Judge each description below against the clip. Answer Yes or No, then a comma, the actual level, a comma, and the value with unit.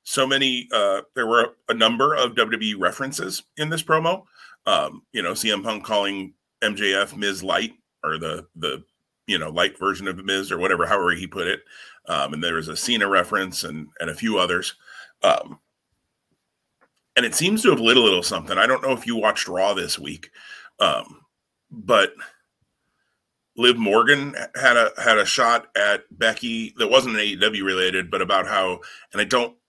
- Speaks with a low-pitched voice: Yes, low, 110 Hz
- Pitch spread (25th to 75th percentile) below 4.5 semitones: No, average, 5.2 semitones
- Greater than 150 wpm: Yes, average, 180 wpm